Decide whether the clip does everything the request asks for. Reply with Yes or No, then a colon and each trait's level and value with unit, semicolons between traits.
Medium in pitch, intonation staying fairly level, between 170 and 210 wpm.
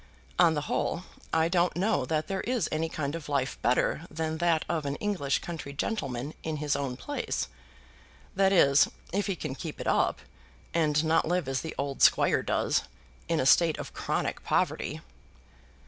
No: medium, 160 Hz; average, 3.4 semitones; average, 180 wpm